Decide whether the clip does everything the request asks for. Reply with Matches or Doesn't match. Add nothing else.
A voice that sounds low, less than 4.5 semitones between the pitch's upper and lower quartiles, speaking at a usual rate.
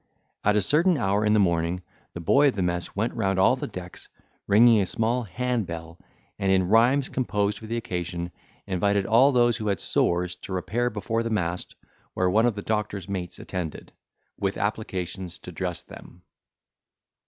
Matches